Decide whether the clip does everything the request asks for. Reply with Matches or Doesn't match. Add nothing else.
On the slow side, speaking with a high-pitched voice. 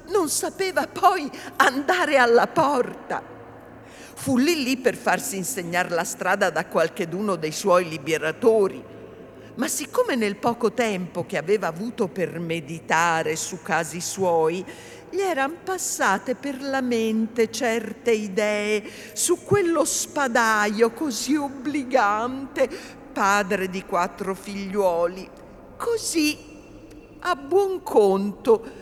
Matches